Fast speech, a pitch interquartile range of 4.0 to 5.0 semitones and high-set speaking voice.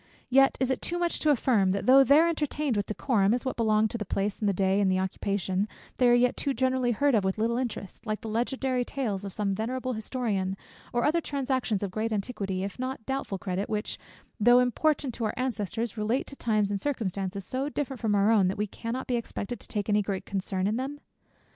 Yes: fast, 225 wpm; average, 4.4 semitones; high, 225 Hz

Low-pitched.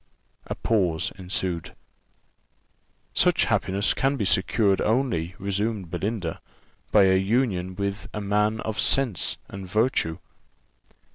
Yes: low, 100 Hz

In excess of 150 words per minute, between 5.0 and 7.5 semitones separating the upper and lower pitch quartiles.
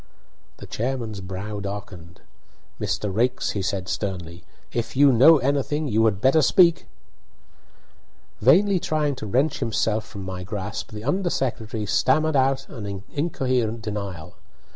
No: slow, 135 wpm; average, 5.3 semitones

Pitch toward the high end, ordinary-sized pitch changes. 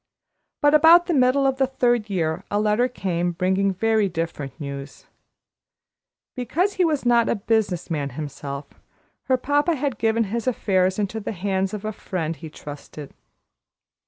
No: high, 210 Hz; wide, 6.6 semitones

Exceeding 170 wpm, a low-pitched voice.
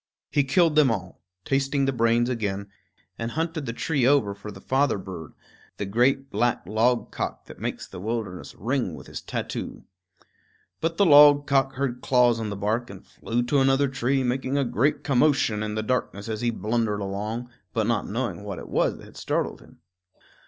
Yes: average, 185 wpm; low, 120 Hz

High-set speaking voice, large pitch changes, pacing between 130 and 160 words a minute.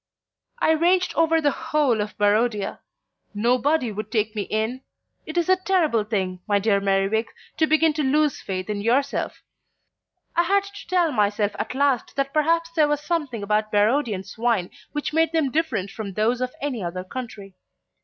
No: very high, 250 Hz; wide, 7.0 semitones; average, 175 wpm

